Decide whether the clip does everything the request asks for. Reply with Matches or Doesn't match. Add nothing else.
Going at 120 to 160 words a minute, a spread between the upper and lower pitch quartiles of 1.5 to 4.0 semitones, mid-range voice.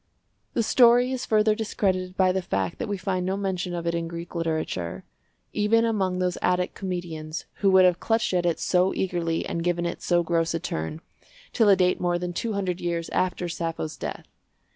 Doesn't match